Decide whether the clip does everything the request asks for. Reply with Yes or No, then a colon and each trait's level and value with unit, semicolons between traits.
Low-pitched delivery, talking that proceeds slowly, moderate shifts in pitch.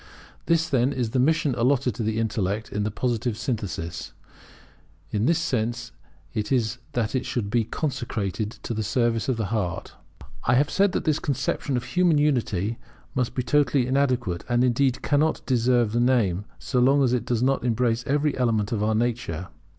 No: low, 120 Hz; average, 180 wpm; average, 3.4 semitones